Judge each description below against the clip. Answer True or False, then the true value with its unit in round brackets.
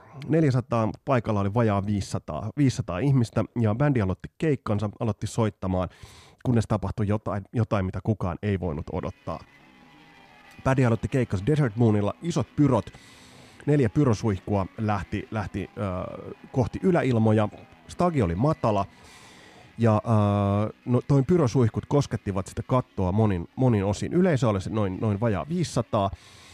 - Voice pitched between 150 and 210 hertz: False (110 Hz)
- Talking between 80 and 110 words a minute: False (130 wpm)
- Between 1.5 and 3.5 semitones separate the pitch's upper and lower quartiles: False (4.2 semitones)